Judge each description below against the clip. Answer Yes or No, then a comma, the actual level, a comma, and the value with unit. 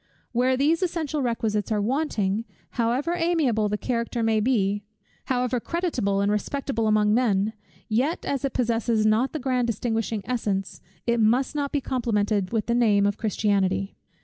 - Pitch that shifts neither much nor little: Yes, average, 3.8 semitones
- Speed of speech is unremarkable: Yes, average, 155 wpm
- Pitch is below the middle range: No, high, 230 Hz